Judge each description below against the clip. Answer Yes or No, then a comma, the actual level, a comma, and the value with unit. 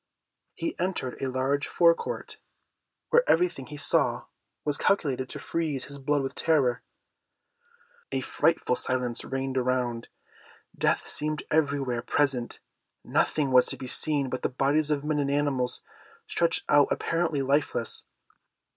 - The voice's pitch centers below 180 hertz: Yes, medium, 140 Hz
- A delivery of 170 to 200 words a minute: No, average, 140 wpm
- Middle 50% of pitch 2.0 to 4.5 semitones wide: Yes, average, 2.8 semitones